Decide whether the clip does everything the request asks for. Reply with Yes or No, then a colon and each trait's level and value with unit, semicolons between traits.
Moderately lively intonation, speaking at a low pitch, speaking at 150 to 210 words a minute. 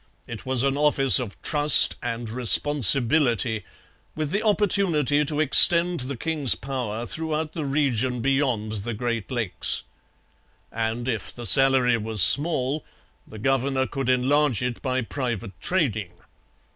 No: average, 3.9 semitones; low, 130 Hz; slow, 135 wpm